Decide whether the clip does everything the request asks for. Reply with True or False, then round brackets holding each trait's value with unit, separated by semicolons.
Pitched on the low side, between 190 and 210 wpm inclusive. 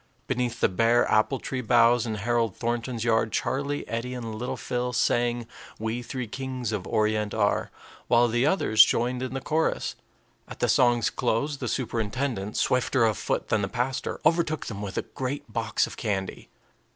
False (120 Hz; 175 wpm)